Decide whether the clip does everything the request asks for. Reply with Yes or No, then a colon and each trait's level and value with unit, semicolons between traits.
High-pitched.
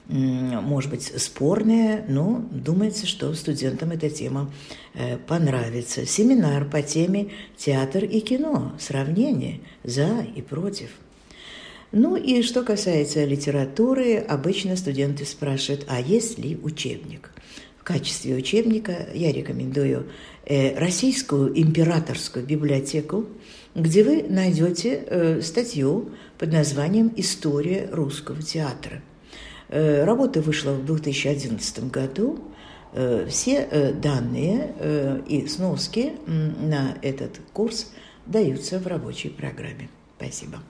No: medium, 155 Hz